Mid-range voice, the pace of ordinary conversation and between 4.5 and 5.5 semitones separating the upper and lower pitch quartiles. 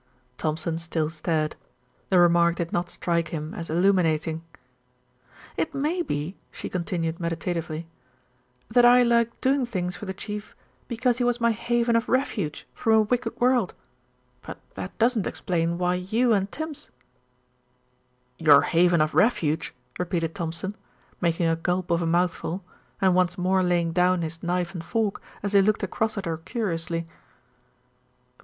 Yes: medium, 180 Hz; average, 155 wpm; average, 4.9 semitones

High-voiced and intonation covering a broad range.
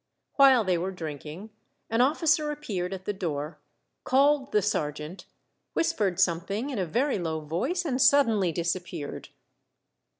Yes: high, 195 Hz; wide, 8.0 semitones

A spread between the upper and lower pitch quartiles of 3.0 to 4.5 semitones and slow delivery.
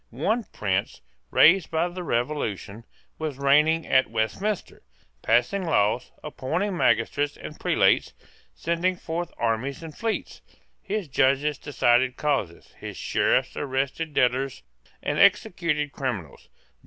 No: average, 5.0 semitones; slow, 115 wpm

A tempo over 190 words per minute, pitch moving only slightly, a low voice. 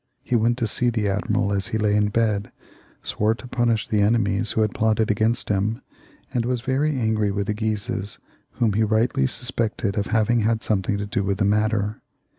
Yes: average, 200 wpm; narrow, 2.0 semitones; low, 110 Hz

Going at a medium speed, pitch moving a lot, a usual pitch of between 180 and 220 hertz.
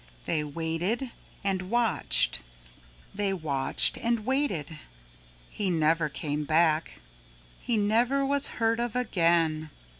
No: slow, 110 wpm; wide, 6.9 semitones; medium, 185 Hz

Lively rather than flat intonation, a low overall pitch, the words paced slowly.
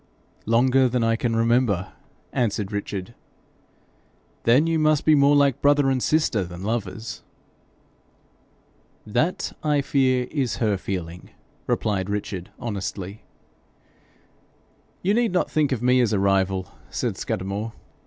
Yes: wide, 5.8 semitones; low, 115 Hz; slow, 125 wpm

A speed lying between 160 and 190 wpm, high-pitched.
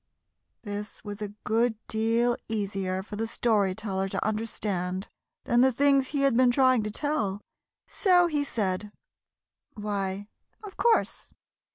No: average, 140 wpm; high, 220 Hz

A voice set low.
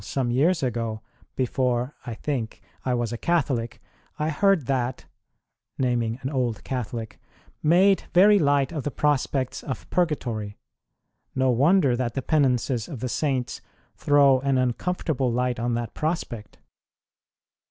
Yes: low, 130 Hz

